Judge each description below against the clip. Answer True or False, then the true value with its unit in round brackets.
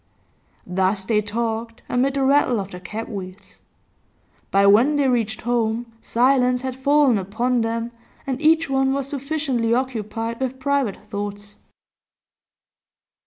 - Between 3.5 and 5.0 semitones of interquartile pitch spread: True (3.9 semitones)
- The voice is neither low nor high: False (235 Hz)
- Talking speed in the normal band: False (130 wpm)